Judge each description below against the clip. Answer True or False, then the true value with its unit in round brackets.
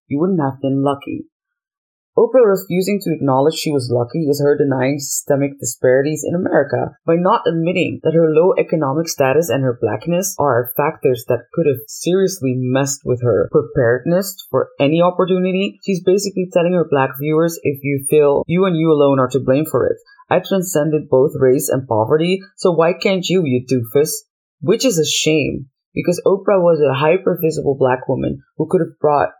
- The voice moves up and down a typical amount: True (5.0 semitones)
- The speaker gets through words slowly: False (180 wpm)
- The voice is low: False (155 Hz)